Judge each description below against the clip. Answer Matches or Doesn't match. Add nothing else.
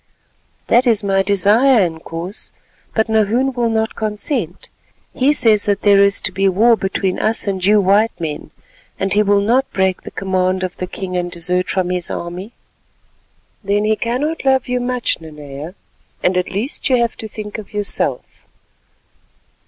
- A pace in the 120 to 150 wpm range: Doesn't match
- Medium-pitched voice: Doesn't match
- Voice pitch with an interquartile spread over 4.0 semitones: Doesn't match